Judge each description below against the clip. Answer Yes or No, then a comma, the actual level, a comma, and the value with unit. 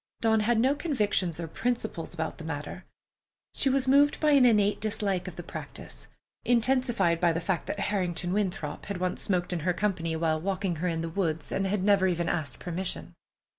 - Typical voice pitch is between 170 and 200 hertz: Yes, medium, 185 Hz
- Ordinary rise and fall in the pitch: Yes, average, 4.4 semitones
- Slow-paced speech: No, average, 200 wpm